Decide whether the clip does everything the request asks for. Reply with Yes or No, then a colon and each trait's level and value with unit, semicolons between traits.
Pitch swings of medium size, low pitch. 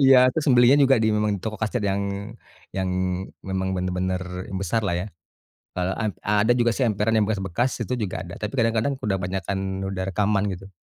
Yes: average, 3.3 semitones; low, 105 Hz